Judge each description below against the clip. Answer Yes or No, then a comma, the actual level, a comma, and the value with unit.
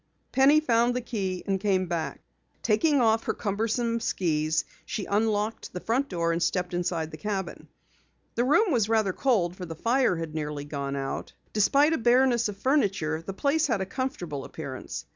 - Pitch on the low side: No, high, 205 Hz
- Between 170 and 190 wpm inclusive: Yes, average, 180 wpm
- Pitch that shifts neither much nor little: No, wide, 6.0 semitones